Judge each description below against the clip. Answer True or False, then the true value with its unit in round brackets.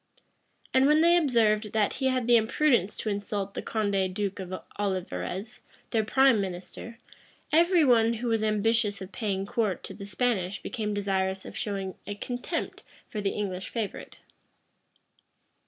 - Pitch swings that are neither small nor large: True (3.4 semitones)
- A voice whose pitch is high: True (210 Hz)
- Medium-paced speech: True (155 wpm)